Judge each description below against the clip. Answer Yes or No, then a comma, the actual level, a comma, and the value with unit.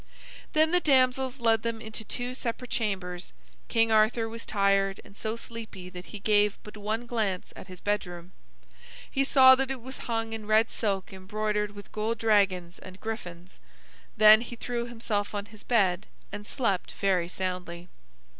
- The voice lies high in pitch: Yes, high, 215 Hz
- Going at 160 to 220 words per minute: Yes, average, 165 wpm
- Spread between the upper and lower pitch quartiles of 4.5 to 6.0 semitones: No, average, 3.0 semitones